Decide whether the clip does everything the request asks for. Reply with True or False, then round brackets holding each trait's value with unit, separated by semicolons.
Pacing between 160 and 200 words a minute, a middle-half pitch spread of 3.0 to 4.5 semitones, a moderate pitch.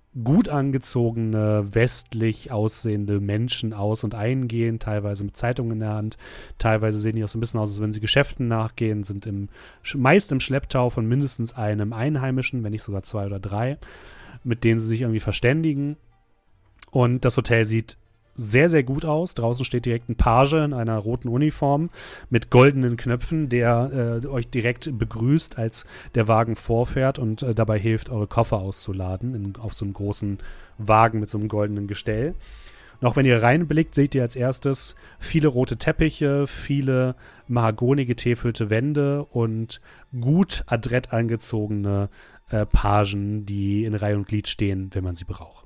False (165 wpm; 3.3 semitones; 115 Hz)